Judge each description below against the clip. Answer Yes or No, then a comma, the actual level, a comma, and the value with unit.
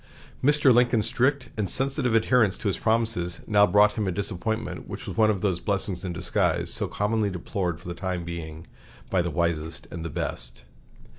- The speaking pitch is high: No, low, 100 Hz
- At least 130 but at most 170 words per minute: No, average, 180 wpm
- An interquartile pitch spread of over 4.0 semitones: Yes, average, 4.5 semitones